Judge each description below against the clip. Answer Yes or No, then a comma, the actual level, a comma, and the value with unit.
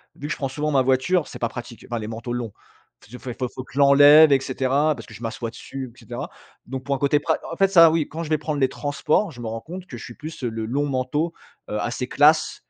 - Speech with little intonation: No, average, 3.8 semitones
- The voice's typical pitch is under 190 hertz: Yes, low, 135 Hz